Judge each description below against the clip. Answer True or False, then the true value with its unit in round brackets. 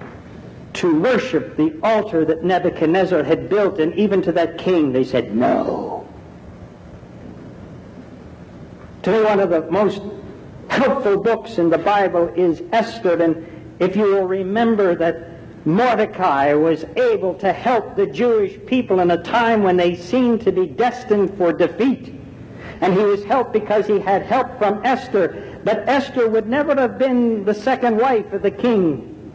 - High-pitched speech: True (195 Hz)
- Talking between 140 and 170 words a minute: True (155 wpm)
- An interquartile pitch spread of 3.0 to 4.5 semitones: False (5.1 semitones)